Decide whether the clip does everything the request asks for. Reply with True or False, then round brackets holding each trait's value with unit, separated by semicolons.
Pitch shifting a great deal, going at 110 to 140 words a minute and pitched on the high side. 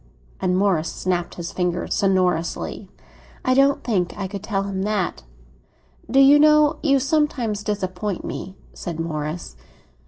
True (6.3 semitones; 135 wpm; 195 Hz)